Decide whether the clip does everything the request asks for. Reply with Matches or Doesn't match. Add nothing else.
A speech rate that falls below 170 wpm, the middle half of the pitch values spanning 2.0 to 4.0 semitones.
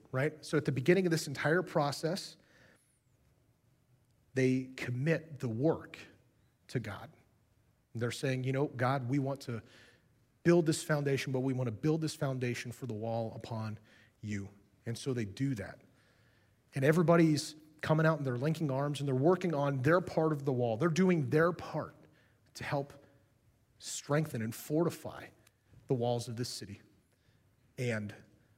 Doesn't match